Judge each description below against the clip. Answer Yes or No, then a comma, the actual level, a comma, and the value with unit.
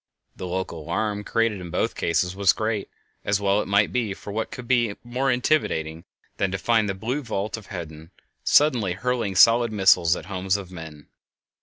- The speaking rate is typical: Yes, average, 190 wpm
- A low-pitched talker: Yes, low, 100 Hz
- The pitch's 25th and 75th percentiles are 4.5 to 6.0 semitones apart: No, average, 3.9 semitones